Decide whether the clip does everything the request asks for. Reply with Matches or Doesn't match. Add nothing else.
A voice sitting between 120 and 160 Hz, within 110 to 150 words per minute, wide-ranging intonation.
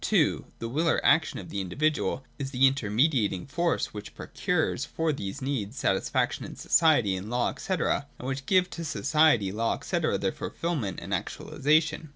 Doesn't match